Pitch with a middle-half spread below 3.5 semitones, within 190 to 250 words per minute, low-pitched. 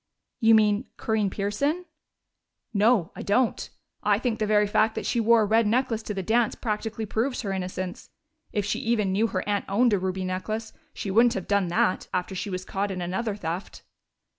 No: average, 2.8 semitones; average, 195 wpm; high, 210 Hz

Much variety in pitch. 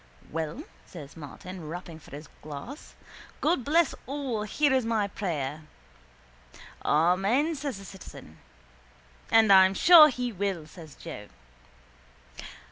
Yes: wide, 8.4 semitones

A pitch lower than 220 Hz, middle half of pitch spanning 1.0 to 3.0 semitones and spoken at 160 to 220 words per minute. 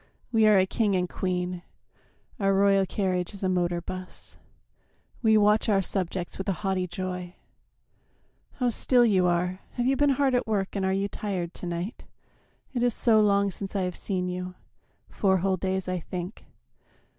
Yes: high, 190 Hz; narrow, 2.4 semitones; average, 180 wpm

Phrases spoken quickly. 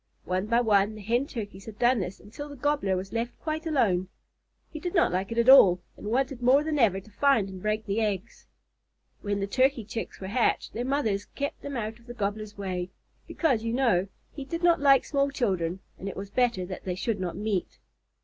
Yes: fast, 220 wpm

